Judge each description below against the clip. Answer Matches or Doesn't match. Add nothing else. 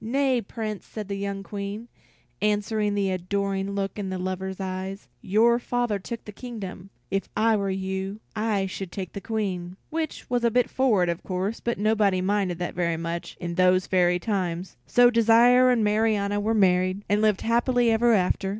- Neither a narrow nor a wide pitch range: Matches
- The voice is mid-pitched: Doesn't match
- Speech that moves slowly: Doesn't match